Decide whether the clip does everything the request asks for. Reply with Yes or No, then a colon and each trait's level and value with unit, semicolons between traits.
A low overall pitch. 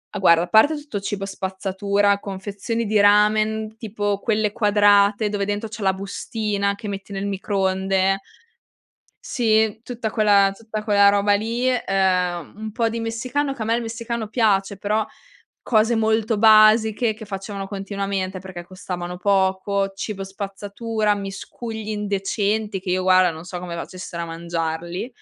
No: high, 205 Hz